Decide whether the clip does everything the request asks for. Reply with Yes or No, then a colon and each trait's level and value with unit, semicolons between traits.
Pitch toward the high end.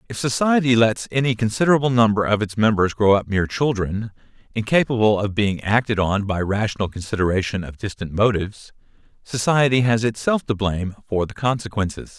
No: low, 110 Hz